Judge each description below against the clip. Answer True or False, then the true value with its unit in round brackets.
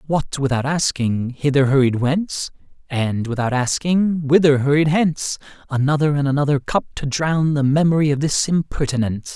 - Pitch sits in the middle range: True (145 Hz)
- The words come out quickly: False (145 wpm)